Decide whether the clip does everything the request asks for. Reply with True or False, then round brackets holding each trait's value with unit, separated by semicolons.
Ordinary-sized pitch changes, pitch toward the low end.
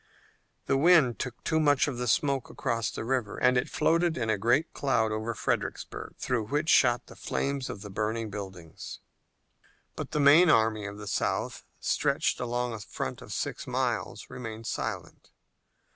True (4.2 semitones; 120 Hz)